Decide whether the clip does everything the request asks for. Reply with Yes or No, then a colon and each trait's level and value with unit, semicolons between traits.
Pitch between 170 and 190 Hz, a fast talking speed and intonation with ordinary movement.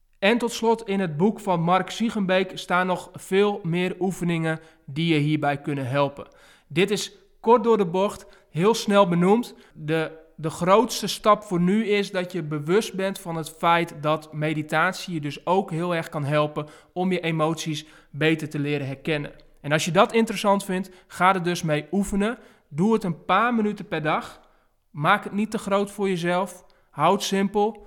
No: medium, 185 Hz; average, 185 wpm; average, 4.0 semitones